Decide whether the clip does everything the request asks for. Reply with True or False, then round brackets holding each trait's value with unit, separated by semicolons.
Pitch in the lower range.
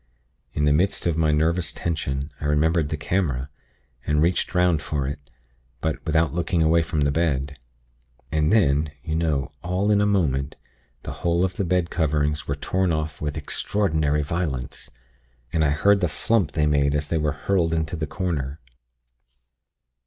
True (80 Hz)